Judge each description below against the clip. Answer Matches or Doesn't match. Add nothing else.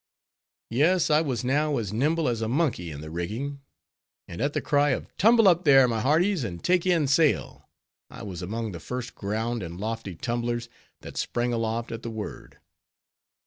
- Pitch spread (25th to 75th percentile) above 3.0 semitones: Matches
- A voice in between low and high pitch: Doesn't match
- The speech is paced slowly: Doesn't match